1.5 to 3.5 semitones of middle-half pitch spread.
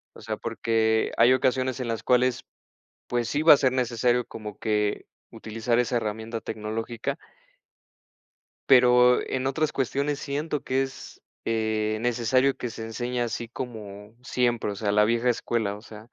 Yes: narrow, 2.4 semitones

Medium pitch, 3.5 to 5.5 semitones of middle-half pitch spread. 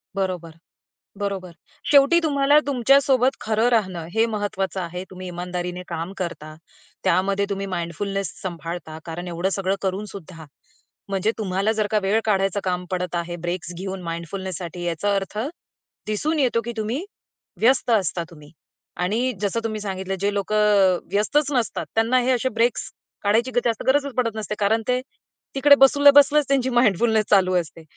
No: high, 200 Hz; average, 4.4 semitones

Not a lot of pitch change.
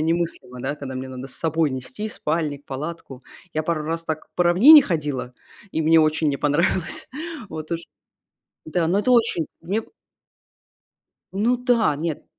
No: average, 3.0 semitones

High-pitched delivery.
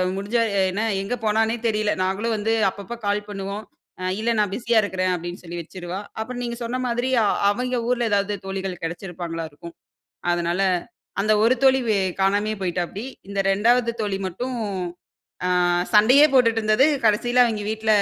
Yes: high, 210 Hz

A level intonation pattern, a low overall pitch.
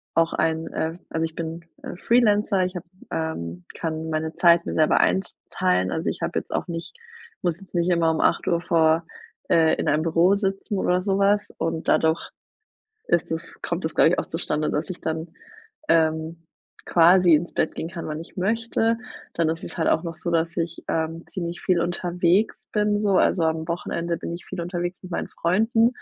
No: narrow, 2.3 semitones; medium, 170 Hz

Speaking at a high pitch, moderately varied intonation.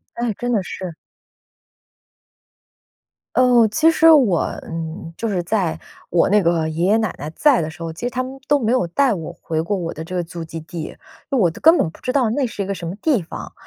No: high, 195 Hz; wide, 6.9 semitones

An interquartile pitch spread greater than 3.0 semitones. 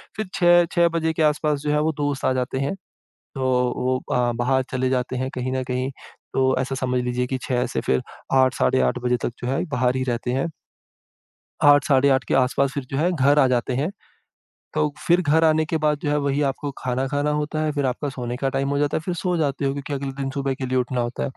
No: average, 2.7 semitones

